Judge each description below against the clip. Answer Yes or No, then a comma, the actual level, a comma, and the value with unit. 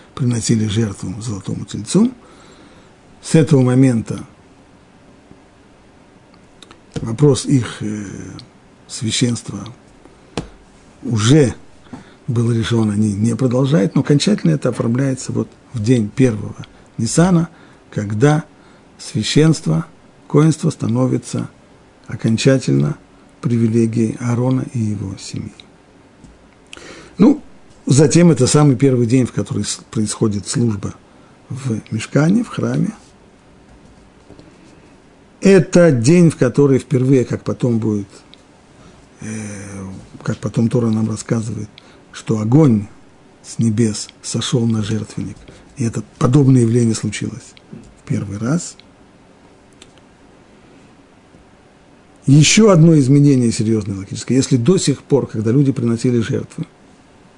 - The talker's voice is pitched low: Yes, low, 120 Hz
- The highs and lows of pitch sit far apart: No, average, 4.5 semitones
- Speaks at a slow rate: Yes, slow, 95 wpm